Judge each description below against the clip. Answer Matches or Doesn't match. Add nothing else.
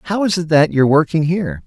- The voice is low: Doesn't match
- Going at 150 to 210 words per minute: Doesn't match